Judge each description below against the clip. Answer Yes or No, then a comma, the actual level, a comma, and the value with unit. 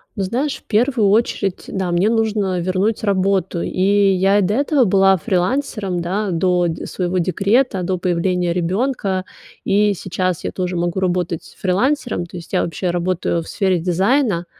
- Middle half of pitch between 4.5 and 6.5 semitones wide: No, average, 2.7 semitones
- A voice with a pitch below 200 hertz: Yes, high, 190 Hz